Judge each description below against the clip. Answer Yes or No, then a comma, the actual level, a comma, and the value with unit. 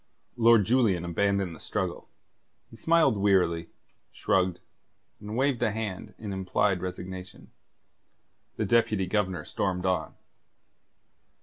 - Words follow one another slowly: Yes, slow, 110 wpm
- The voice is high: No, low, 100 Hz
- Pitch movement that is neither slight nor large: Yes, average, 3.3 semitones